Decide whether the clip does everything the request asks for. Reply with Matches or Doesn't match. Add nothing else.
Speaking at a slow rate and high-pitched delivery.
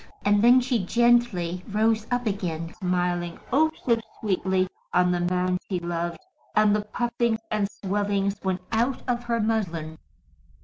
Doesn't match